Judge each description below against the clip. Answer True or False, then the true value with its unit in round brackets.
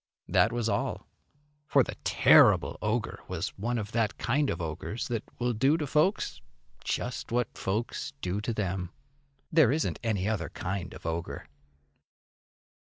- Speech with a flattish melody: False (4.1 semitones)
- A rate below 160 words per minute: True (150 wpm)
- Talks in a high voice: False (110 Hz)